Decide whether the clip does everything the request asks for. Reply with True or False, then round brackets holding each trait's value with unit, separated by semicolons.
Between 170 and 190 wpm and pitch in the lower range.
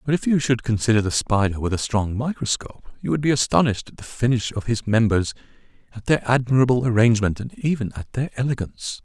False (200 wpm; 115 Hz)